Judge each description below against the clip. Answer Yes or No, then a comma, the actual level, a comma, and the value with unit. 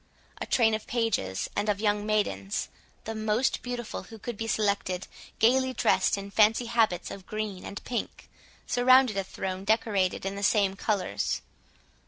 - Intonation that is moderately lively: No, narrow, 2.3 semitones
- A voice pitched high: Yes, high, 215 Hz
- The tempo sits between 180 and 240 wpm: No, average, 160 wpm